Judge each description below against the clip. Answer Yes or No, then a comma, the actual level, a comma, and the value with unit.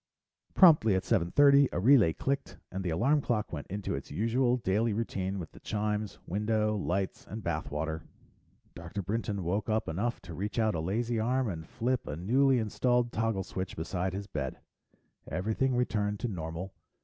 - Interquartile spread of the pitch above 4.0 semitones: Yes, average, 4.5 semitones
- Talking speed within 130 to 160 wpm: No, average, 175 wpm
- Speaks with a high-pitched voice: No, low, 105 Hz